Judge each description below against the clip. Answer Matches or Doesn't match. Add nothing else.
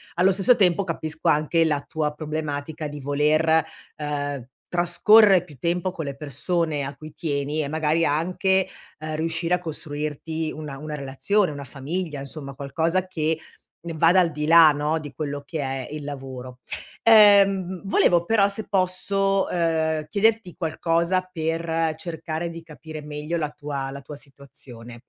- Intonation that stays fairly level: Doesn't match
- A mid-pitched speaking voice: Matches